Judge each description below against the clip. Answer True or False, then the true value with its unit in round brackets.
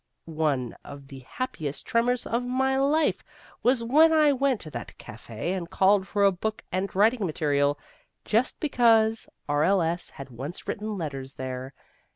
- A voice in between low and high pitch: False (195 Hz)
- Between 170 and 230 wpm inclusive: False (155 wpm)